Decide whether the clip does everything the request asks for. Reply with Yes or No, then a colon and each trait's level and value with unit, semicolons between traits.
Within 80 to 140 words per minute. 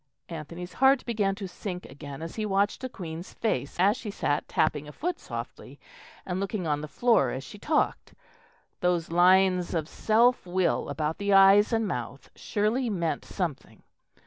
No: average, 170 wpm